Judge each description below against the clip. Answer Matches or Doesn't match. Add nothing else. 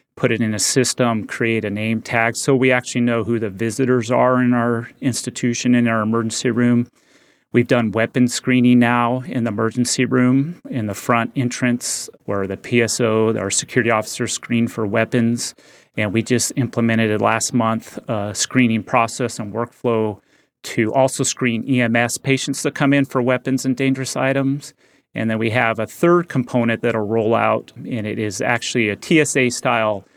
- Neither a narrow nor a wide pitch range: Doesn't match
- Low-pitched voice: Matches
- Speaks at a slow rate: Doesn't match